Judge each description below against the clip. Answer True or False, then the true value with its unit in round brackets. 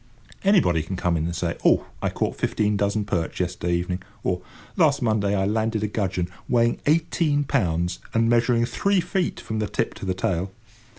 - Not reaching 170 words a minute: False (185 wpm)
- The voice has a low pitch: True (100 Hz)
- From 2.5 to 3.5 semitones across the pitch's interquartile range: False (4.7 semitones)